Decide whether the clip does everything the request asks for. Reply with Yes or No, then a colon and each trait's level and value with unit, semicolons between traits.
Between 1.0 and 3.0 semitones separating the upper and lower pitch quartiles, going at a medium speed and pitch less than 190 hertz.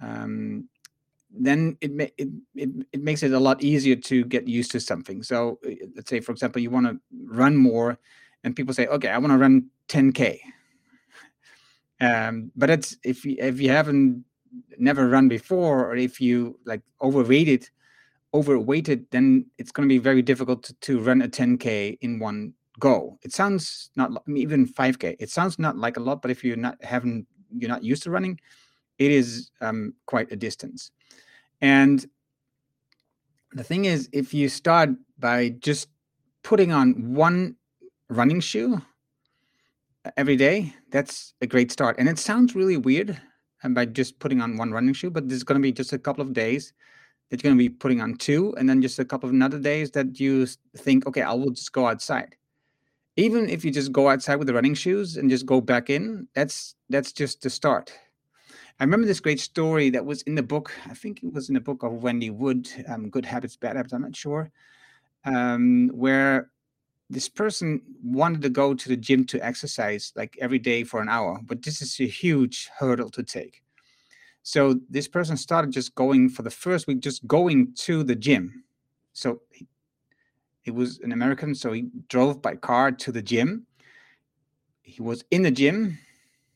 Yes: average, 2.7 semitones; average, 190 wpm; low, 135 Hz